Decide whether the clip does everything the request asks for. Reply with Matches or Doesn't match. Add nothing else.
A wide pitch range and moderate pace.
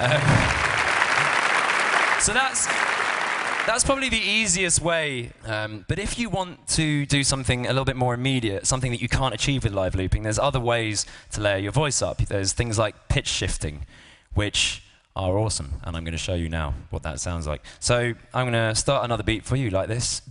Doesn't match